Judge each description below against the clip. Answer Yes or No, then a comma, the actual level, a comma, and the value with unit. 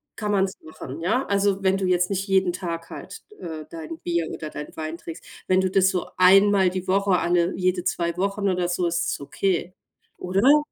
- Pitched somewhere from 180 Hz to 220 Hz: Yes, medium, 185 Hz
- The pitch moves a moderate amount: No, narrow, 2.3 semitones